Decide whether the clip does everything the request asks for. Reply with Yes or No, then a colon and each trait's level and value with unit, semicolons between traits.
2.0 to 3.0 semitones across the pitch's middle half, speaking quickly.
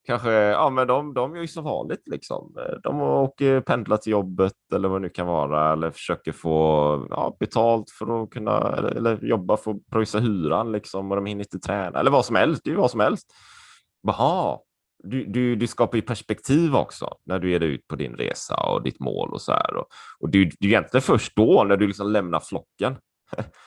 No: average, 3.7 semitones; fast, 225 wpm